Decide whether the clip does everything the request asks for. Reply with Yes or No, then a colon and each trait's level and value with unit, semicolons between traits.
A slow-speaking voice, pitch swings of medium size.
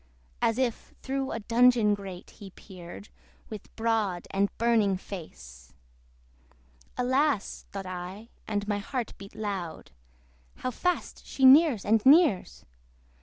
Yes: slow, 125 wpm; average, 4.3 semitones